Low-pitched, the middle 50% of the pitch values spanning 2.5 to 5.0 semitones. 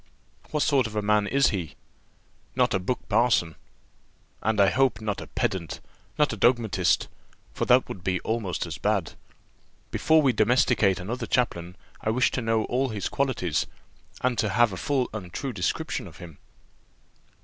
Yes: low, 110 Hz; average, 4.7 semitones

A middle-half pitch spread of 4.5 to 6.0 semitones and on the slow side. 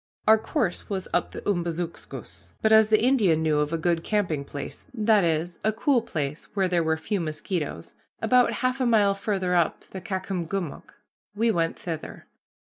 No: average, 5.1 semitones; average, 175 wpm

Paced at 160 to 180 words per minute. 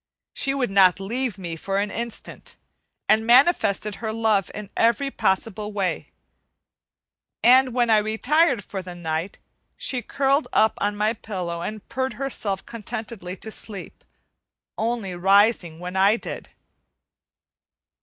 No: slow, 135 wpm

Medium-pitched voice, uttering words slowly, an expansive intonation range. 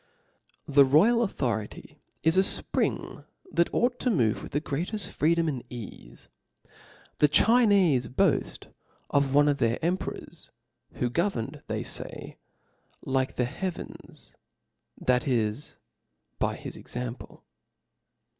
Yes: medium, 145 Hz; slow, 120 wpm; wide, 6.7 semitones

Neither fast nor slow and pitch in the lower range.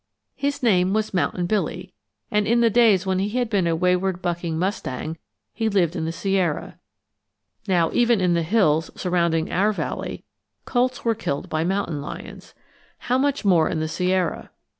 No: average, 170 wpm; medium, 185 Hz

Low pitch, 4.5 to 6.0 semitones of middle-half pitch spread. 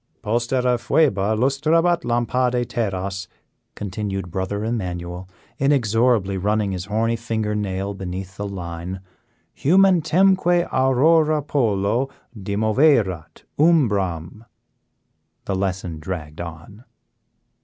Yes: low, 105 Hz; wide, 5.5 semitones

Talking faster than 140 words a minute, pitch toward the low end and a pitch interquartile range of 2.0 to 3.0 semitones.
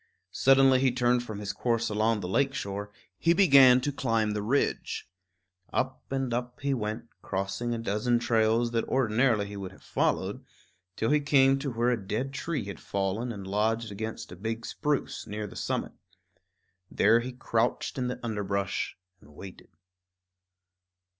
No: average, 165 wpm; low, 115 Hz; average, 3.7 semitones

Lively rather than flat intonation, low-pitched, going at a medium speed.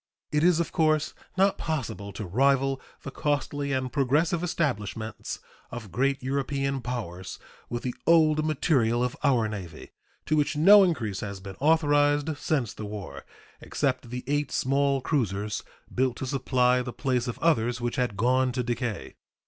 No: average, 3.8 semitones; low, 130 Hz; average, 155 wpm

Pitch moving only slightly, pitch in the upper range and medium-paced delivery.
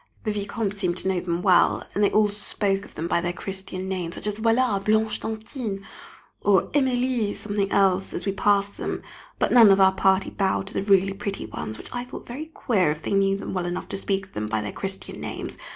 No: narrow, 1.9 semitones; high, 195 Hz; fast, 230 wpm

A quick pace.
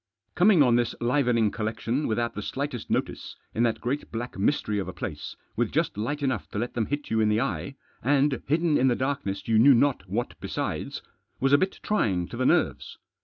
Yes: fast, 210 wpm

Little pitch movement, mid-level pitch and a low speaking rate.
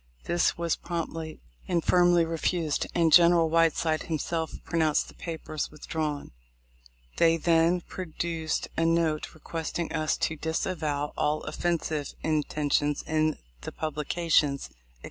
Yes: narrow, 1.6 semitones; medium, 160 Hz; slow, 120 wpm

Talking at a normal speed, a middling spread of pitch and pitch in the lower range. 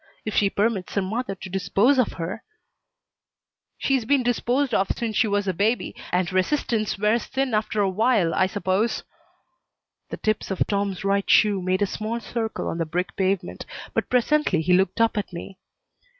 No: average, 180 wpm; average, 3.4 semitones; high, 205 Hz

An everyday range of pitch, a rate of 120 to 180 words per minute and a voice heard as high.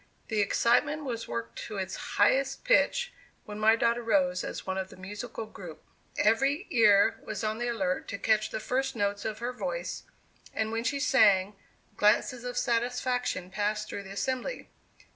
Yes: average, 3.6 semitones; average, 170 wpm; high, 220 Hz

